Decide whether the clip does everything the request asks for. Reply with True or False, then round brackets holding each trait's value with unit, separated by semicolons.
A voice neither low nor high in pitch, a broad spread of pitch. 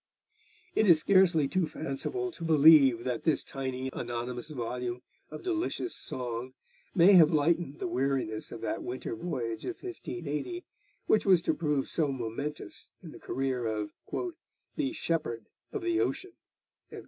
True (150 Hz; 6.3 semitones)